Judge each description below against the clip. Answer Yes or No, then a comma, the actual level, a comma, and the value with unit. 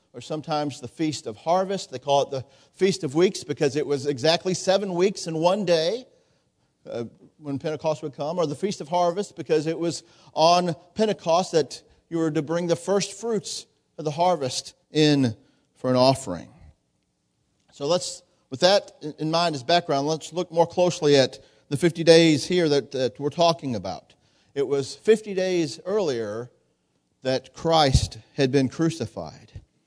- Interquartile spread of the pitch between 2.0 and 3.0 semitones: No, average, 4.1 semitones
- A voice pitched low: No, medium, 160 Hz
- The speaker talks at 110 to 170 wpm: Yes, average, 165 wpm